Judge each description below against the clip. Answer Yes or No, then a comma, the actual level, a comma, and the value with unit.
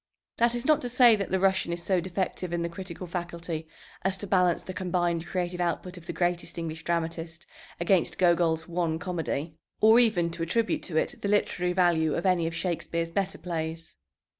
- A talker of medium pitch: Yes, medium, 175 Hz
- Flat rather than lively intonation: Yes, narrow, 2.1 semitones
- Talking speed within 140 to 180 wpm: No, average, 190 wpm